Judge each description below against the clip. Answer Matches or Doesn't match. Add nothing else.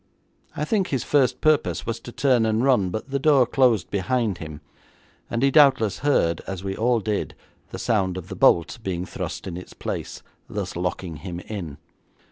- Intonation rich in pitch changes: Matches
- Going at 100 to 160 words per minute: Doesn't match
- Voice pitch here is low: Matches